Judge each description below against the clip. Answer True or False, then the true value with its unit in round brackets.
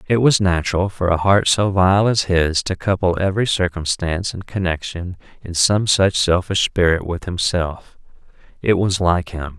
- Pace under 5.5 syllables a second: True (4.7 syllables/s)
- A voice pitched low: True (90 Hz)